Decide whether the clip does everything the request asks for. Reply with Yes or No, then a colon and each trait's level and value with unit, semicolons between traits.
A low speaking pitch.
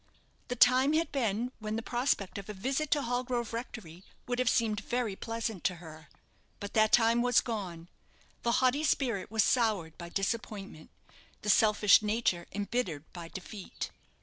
No: high, 220 Hz